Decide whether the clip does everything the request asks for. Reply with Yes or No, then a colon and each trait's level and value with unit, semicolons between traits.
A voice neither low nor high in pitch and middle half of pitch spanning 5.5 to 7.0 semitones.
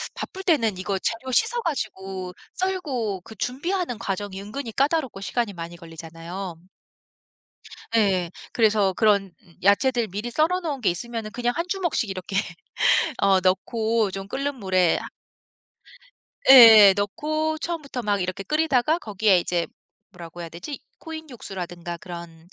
No: high, 215 Hz; wide, 6.2 semitones